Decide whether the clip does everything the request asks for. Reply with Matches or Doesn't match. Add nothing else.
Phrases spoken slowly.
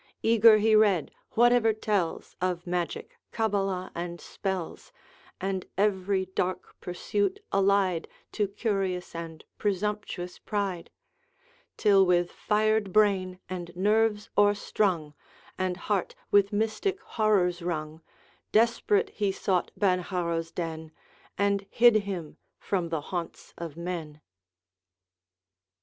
Matches